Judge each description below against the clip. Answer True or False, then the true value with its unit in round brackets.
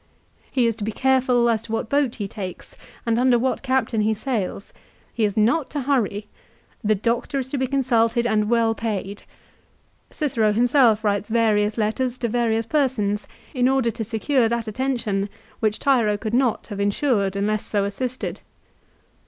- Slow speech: False (170 wpm)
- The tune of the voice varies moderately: True (3.3 semitones)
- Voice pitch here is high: True (230 Hz)